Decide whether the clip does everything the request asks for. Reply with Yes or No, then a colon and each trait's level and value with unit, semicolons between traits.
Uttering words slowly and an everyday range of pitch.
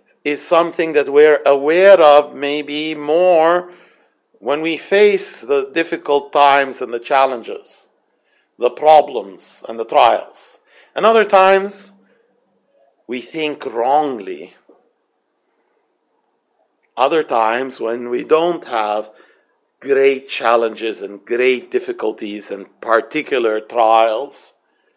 No: slow, 100 wpm; wide, 7.2 semitones